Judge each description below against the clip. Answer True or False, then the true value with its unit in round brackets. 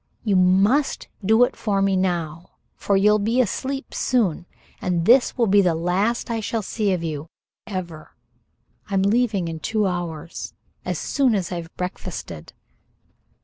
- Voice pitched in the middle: False (195 Hz)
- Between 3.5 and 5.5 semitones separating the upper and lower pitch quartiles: True (4.1 semitones)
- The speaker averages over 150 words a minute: False (145 wpm)